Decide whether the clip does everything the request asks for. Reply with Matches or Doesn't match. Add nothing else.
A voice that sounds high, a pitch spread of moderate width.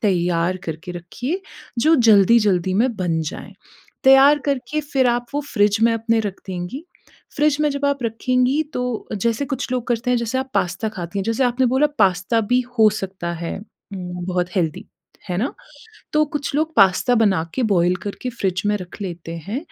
Doesn't match